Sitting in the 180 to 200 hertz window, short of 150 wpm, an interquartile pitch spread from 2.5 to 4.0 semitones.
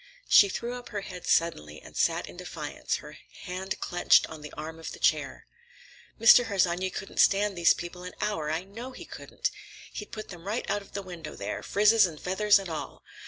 No: high, 190 Hz; fast, 205 wpm; average, 3.5 semitones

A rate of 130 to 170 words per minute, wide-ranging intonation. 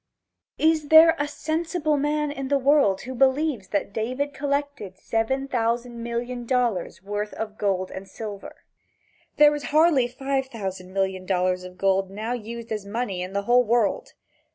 Yes: average, 160 wpm; wide, 6.0 semitones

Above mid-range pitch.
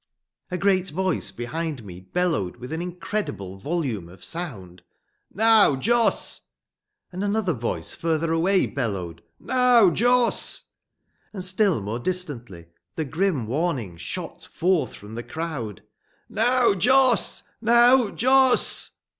No: medium, 170 Hz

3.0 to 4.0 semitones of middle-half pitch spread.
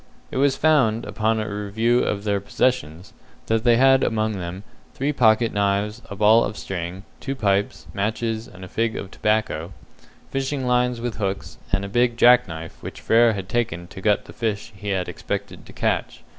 Yes: average, 3.4 semitones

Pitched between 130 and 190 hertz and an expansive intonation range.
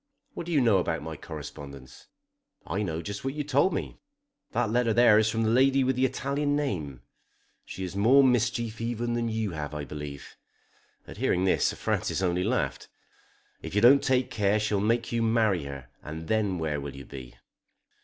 No: low, 110 Hz; wide, 7.0 semitones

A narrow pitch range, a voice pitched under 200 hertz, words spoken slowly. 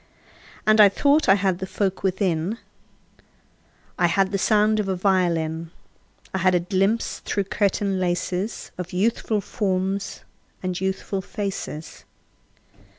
Yes: narrow, 2.0 semitones; high, 190 Hz; slow, 130 wpm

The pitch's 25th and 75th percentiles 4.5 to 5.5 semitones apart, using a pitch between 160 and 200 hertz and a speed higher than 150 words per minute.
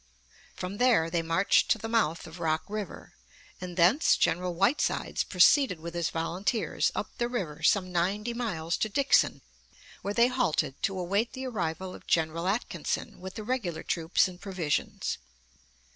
Yes: average, 5.1 semitones; medium, 185 Hz; average, 160 wpm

